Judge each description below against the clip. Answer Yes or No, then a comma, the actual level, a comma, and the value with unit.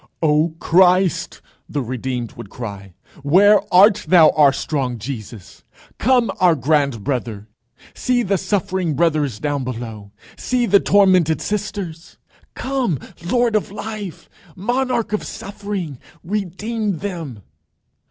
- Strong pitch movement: Yes, wide, 7.0 semitones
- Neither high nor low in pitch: Yes, medium, 175 Hz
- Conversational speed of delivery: No, slow, 115 wpm